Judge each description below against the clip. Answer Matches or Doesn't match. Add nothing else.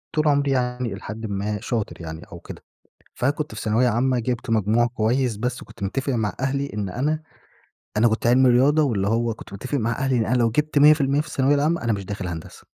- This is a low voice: Matches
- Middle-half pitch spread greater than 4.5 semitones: Doesn't match